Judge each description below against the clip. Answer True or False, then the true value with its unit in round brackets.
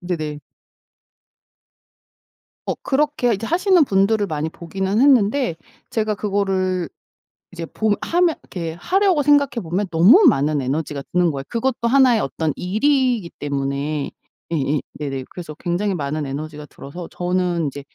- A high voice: False (180 Hz)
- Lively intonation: True (7.4 semitones)